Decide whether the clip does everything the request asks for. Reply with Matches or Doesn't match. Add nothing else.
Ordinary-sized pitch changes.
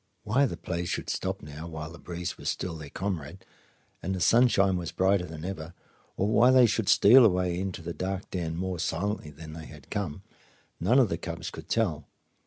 Matches